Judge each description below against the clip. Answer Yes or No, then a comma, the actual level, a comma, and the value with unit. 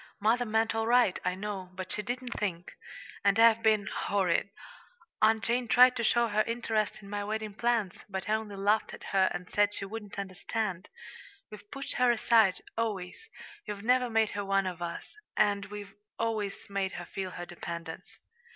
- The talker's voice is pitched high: Yes, high, 210 Hz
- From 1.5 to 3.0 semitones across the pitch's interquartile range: Yes, narrow, 2.6 semitones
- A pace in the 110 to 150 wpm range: No, average, 180 wpm